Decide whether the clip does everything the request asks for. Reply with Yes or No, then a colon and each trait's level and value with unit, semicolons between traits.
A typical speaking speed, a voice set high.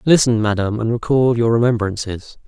No: average, 145 wpm; low, 115 Hz